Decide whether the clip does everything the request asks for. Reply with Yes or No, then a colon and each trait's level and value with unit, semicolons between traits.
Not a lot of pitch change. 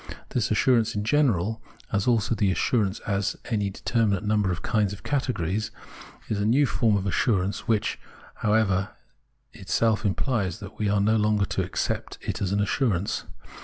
Yes: narrow, 2.2 semitones